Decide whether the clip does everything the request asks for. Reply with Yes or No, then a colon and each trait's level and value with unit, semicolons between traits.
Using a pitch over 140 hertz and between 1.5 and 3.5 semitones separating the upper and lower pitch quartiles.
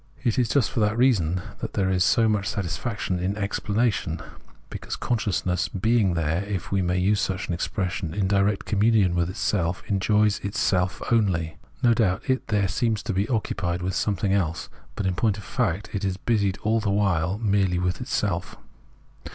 No: low, 100 Hz; average, 2.9 semitones